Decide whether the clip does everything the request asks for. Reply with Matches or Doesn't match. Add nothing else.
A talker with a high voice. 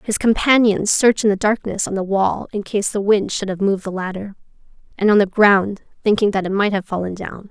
Matches